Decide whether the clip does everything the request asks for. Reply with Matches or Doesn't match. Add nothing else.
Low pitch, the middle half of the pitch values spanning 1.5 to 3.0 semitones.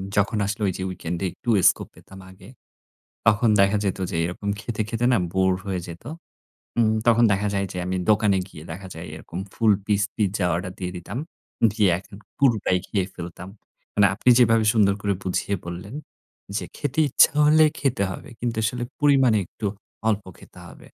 Doesn't match